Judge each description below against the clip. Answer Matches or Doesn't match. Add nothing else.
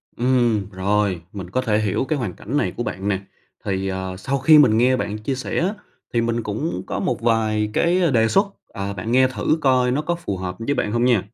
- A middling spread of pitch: Matches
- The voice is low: Matches